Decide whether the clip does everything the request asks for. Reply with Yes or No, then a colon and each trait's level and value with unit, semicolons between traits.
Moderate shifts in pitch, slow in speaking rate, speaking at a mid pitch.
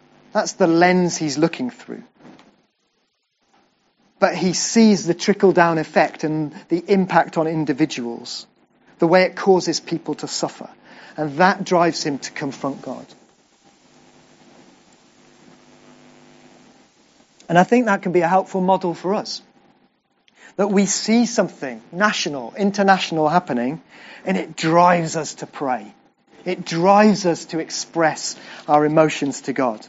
Yes: average, 3.6 semitones; slow, 130 wpm; medium, 170 Hz